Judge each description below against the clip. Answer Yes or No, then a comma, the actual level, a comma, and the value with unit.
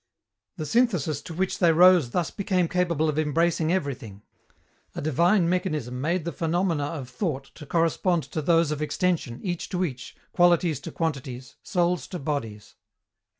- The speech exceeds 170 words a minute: No, average, 155 wpm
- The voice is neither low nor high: Yes, medium, 165 Hz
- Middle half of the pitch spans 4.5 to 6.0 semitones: No, average, 3.8 semitones